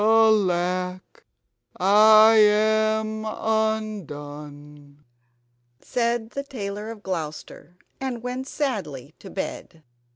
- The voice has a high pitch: Yes, high, 215 Hz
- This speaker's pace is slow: Yes, slow, 85 wpm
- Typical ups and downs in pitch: Yes, average, 3.9 semitones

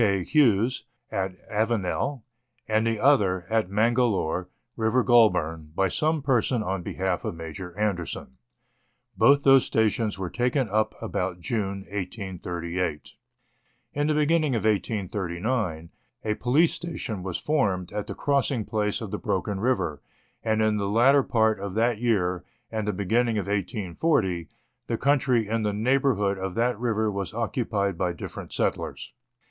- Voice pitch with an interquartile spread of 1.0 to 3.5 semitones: No, average, 4.3 semitones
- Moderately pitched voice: No, low, 105 Hz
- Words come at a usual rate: Yes, average, 150 wpm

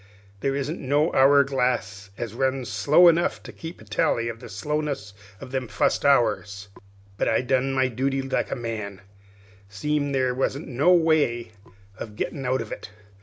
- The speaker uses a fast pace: No, average, 170 wpm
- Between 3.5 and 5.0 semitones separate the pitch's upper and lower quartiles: Yes, average, 3.9 semitones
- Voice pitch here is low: Yes, low, 130 Hz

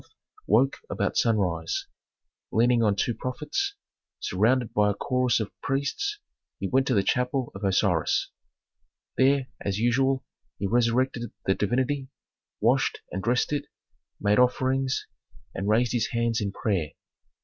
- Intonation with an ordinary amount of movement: Yes, average, 4.3 semitones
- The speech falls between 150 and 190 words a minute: No, slow, 135 wpm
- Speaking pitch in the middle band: No, low, 120 Hz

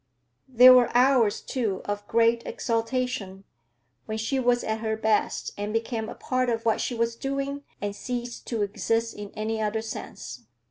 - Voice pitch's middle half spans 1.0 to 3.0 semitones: Yes, narrow, 2.4 semitones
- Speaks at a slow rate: No, average, 170 wpm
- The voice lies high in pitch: Yes, high, 230 Hz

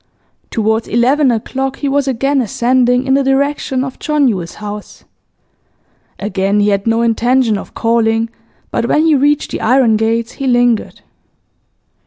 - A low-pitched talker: No, high, 240 Hz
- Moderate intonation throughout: Yes, average, 3.3 semitones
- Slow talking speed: No, average, 150 wpm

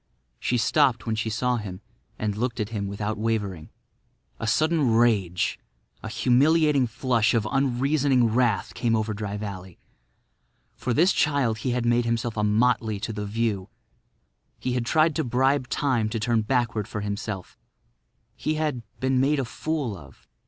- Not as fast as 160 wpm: Yes, average, 150 wpm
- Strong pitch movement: No, average, 3.3 semitones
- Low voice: Yes, low, 115 Hz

